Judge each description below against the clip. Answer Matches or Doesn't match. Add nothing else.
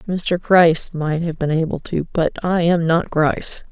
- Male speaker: Doesn't match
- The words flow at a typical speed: Matches